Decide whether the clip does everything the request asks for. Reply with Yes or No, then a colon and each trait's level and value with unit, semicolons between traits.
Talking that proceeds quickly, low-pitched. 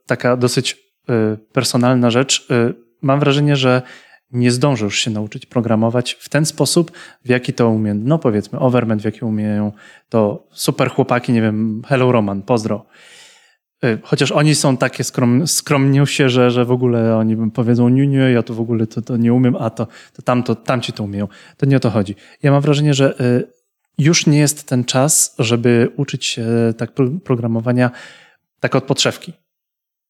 Yes: fast, 170 wpm; low, 125 Hz